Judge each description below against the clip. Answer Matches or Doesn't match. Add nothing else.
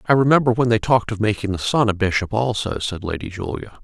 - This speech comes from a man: Matches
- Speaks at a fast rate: Matches